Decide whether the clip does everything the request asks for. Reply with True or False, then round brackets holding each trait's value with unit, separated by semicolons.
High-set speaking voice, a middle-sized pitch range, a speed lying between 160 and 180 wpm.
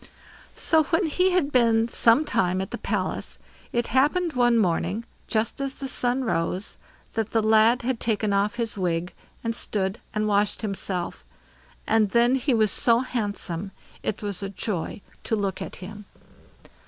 True (220 Hz; 3.5 semitones; 165 wpm)